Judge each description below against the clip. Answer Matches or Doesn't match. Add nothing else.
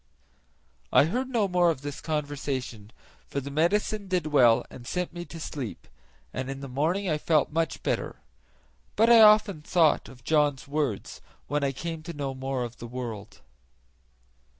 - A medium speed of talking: Matches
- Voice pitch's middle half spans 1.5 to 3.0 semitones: Doesn't match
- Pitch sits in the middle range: Matches